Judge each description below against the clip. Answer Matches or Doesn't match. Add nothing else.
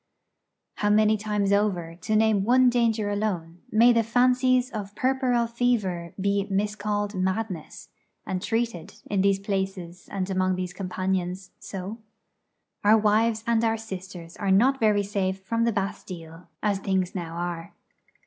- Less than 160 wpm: Matches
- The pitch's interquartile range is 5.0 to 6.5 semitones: Doesn't match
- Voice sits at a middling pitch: Doesn't match